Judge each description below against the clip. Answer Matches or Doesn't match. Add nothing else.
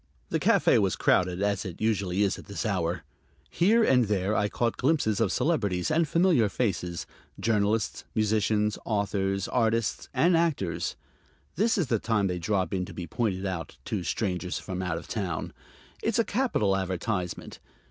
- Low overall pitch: Matches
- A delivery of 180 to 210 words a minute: Doesn't match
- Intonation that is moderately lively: Matches